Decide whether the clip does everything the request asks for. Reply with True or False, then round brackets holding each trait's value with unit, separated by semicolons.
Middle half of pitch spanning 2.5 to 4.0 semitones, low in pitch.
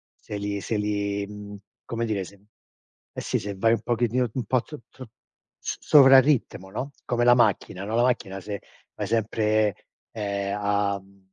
True (2.9 semitones; 105 Hz)